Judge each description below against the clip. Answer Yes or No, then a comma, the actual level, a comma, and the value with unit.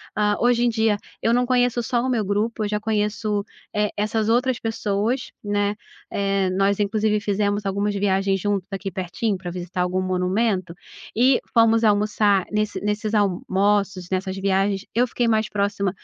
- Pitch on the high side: Yes, high, 205 Hz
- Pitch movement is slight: Yes, narrow, 2.2 semitones